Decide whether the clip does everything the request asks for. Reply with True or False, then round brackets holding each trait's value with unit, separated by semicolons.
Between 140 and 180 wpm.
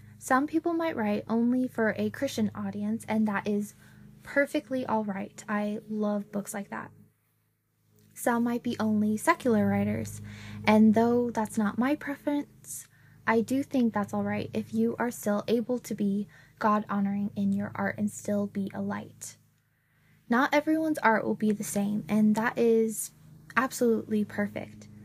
True (155 wpm)